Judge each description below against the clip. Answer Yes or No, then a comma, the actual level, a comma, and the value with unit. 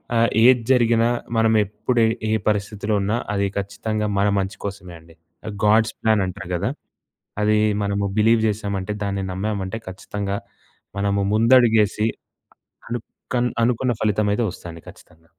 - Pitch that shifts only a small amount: Yes, narrow, 2.2 semitones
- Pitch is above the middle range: No, low, 105 Hz